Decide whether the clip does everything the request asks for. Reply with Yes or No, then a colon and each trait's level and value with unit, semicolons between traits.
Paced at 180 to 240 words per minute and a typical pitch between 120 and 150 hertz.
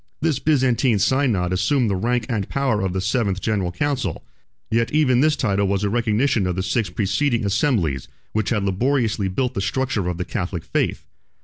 No: average, 185 wpm; low, 110 Hz